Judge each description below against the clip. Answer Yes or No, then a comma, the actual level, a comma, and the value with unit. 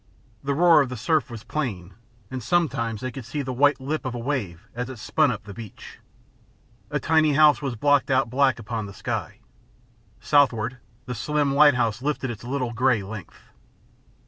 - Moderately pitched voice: No, low, 130 Hz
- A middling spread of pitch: Yes, average, 3.9 semitones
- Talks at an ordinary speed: Yes, average, 180 wpm